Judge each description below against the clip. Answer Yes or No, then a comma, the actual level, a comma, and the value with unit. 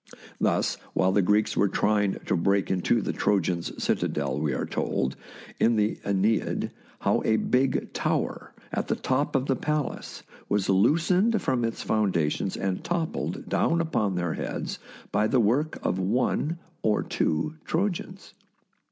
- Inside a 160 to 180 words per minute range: No, average, 150 wpm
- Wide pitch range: Yes, wide, 7.3 semitones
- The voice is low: Yes, low, 110 Hz